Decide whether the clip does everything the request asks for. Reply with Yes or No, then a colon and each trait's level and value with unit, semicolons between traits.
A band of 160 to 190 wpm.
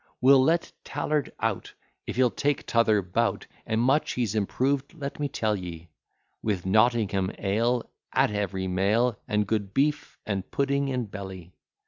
No: average, 150 wpm